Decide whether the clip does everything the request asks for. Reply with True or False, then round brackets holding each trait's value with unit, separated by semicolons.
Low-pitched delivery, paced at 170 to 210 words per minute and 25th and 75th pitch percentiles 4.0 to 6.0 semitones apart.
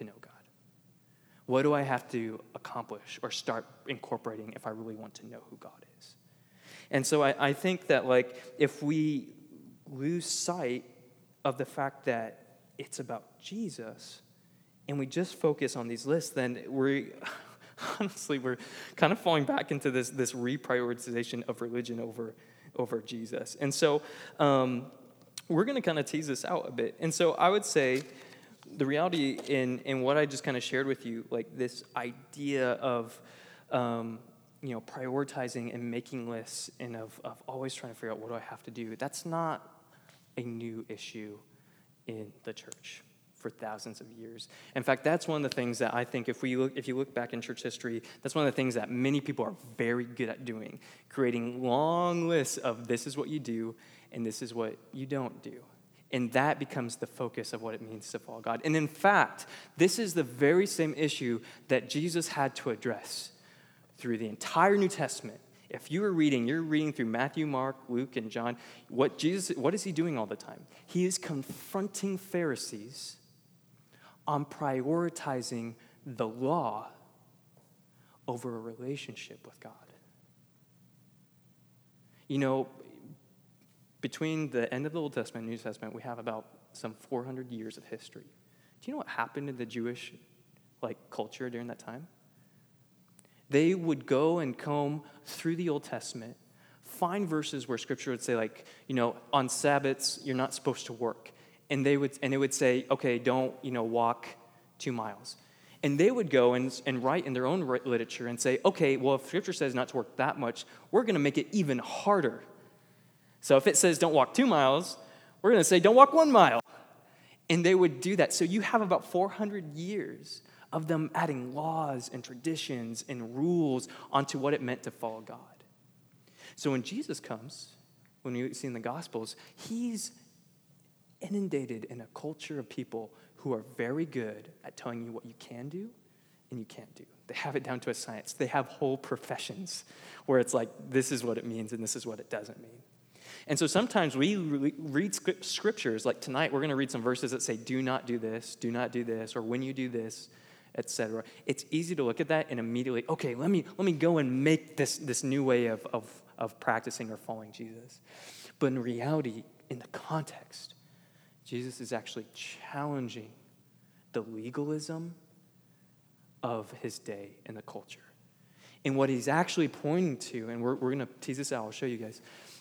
True (130 Hz; 185 wpm; 4.6 semitones)